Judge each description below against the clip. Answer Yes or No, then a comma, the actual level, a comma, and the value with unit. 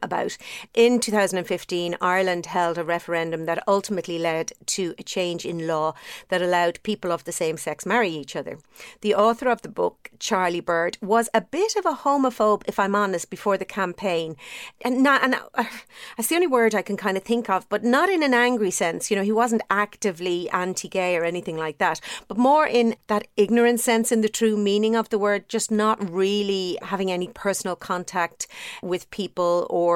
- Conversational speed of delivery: Yes, average, 195 wpm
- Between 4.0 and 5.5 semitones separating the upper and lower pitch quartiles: Yes, average, 4.4 semitones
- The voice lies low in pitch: No, high, 200 Hz